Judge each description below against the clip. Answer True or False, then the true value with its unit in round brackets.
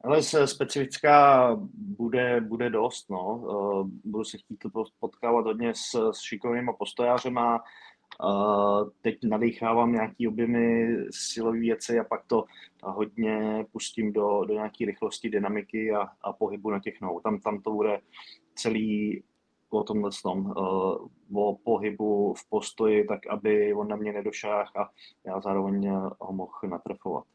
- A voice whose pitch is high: False (110 Hz)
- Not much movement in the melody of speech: True (2.2 semitones)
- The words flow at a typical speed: True (140 wpm)